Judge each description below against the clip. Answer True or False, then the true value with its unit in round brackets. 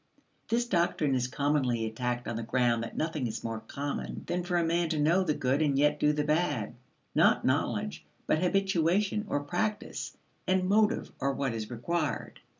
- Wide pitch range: True (5.8 semitones)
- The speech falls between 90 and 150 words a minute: False (180 wpm)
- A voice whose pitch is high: False (150 Hz)